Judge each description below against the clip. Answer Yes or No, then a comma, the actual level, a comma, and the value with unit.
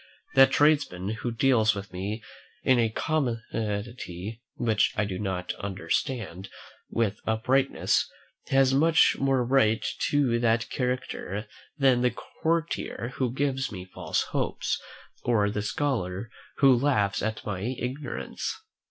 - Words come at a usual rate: No, slow, 125 wpm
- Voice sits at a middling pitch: No, low, 115 Hz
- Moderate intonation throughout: Yes, average, 4.5 semitones